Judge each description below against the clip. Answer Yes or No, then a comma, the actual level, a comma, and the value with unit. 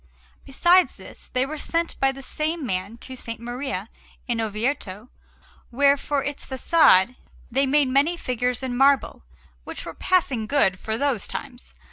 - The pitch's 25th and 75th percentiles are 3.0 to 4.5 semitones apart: Yes, average, 3.4 semitones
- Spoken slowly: No, average, 155 wpm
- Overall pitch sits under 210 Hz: No, very high, 265 Hz